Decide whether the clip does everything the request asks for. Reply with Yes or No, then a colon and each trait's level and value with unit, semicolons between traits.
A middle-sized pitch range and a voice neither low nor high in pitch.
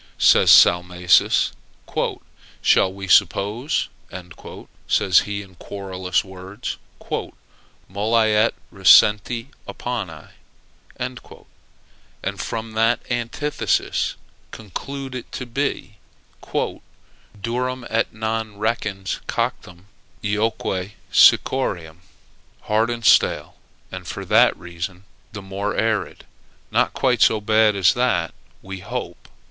No: average, 3.4 semitones; low, 105 Hz